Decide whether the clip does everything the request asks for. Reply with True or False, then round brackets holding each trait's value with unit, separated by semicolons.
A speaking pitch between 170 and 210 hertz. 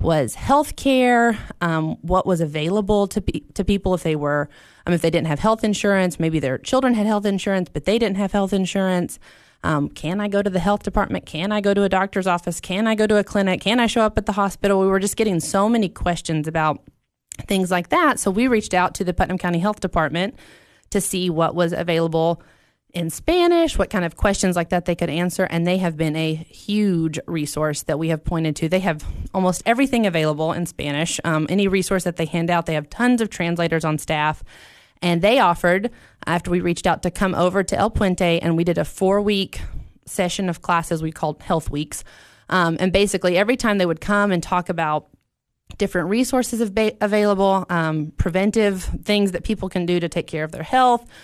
True (185 Hz)